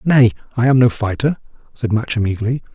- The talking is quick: No, average, 175 wpm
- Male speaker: Yes, male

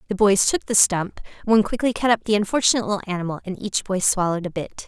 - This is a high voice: Yes, high, 200 Hz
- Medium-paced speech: No, fast, 235 wpm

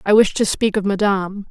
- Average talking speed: No, fast, 240 wpm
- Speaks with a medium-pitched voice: No, high, 200 Hz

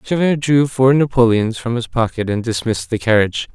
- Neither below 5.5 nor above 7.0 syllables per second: Yes, 5.6 syllables/s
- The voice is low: Yes, low, 120 Hz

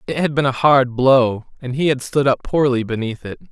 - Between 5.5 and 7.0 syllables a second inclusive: No, 5.1 syllables/s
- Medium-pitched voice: No, low, 130 Hz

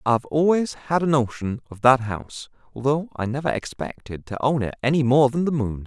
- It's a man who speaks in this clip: Yes, male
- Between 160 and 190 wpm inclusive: No, fast, 205 wpm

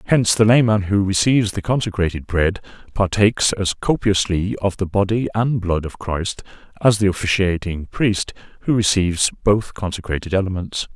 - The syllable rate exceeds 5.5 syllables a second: No, 5.1 syllables/s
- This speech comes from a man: Yes, male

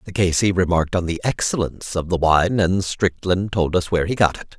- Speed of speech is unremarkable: No, fast, 235 wpm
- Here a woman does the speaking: No, male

